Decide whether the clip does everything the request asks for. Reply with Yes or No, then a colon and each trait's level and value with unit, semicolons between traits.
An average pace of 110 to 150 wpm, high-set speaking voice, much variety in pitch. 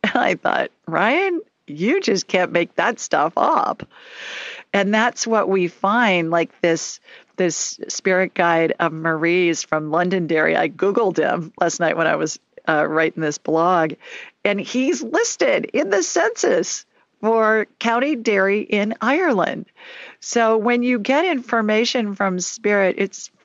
Yes: average, 145 wpm; high, 200 Hz; wide, 5.9 semitones